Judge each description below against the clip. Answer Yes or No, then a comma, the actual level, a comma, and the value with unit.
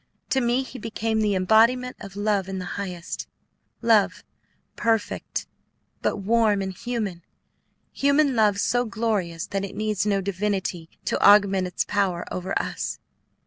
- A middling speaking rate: Yes, average, 145 wpm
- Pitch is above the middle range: Yes, high, 205 Hz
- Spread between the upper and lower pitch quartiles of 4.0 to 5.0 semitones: No, average, 3.0 semitones